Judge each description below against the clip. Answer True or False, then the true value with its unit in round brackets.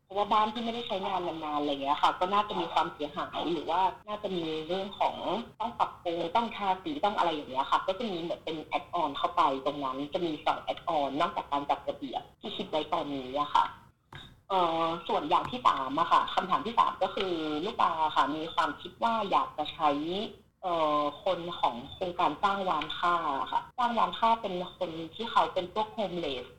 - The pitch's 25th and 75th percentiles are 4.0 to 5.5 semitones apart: True (5.0 semitones)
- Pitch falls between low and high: True (180 Hz)